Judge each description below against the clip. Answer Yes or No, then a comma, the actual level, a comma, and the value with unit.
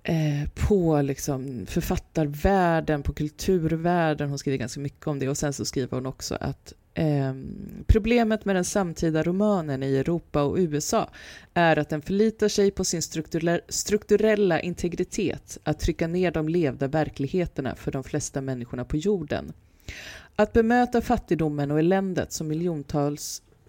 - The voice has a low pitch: No, medium, 155 Hz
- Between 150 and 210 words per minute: No, average, 140 wpm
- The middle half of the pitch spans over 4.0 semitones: Yes, average, 4.7 semitones